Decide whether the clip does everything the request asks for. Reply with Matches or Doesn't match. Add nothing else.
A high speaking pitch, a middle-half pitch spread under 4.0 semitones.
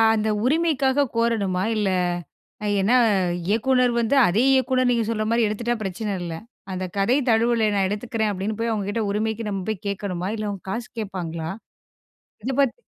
Matches